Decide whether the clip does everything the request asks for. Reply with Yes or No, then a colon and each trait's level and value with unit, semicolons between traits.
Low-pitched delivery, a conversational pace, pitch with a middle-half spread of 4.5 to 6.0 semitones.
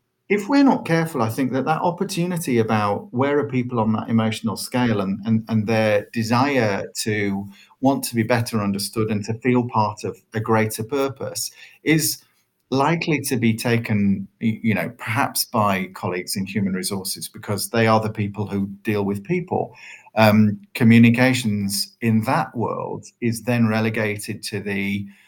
No: low, 110 Hz; average, 160 wpm; average, 3.3 semitones